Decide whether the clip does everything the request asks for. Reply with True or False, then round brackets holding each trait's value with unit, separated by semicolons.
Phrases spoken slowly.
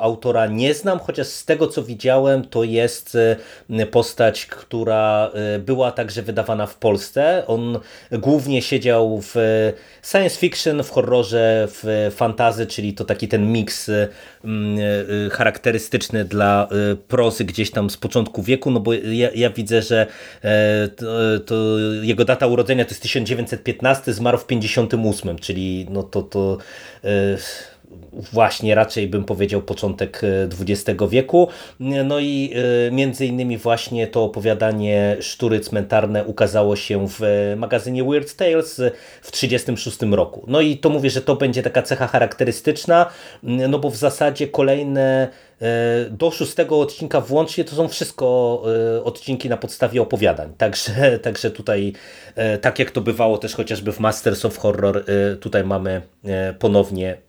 False (135 wpm)